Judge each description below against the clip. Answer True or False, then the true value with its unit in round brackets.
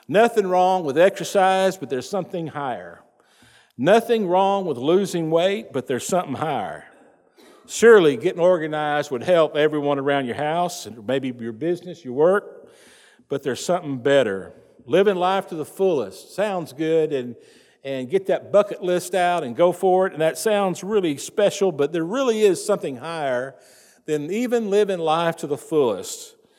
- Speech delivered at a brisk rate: False (165 wpm)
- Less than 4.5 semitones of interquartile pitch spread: False (5.0 semitones)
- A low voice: False (175 Hz)